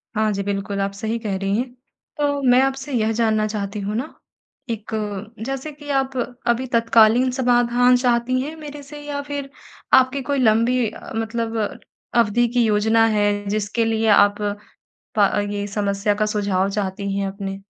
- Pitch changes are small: No, average, 3.7 semitones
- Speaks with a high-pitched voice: Yes, high, 225 Hz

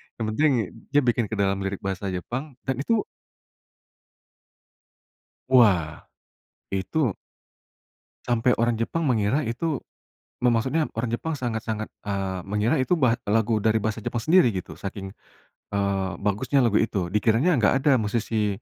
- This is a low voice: Yes, low, 115 Hz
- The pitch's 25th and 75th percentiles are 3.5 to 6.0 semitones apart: Yes, average, 4.2 semitones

